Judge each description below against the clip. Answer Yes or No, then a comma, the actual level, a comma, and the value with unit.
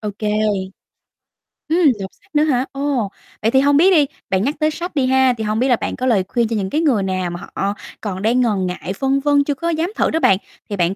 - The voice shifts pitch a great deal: Yes, wide, 6.1 semitones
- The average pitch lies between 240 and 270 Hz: Yes, very high, 250 Hz